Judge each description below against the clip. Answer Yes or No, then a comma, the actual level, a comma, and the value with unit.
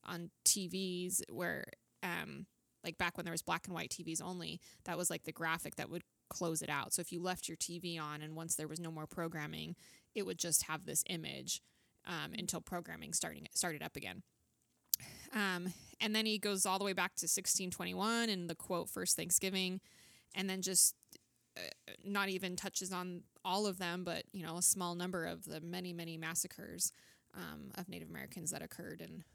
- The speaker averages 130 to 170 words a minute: No, average, 195 wpm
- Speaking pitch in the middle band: Yes, medium, 175 Hz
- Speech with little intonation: Yes, narrow, 2.2 semitones